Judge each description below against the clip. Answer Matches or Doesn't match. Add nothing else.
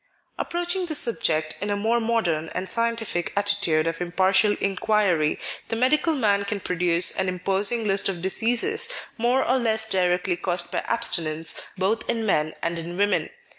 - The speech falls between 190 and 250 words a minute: Doesn't match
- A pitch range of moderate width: Matches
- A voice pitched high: Matches